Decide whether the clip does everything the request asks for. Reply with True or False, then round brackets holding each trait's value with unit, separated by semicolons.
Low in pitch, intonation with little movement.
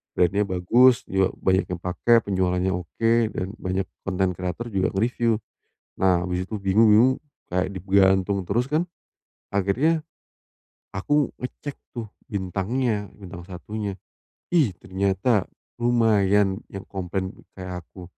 False (95 Hz; 3.5 semitones)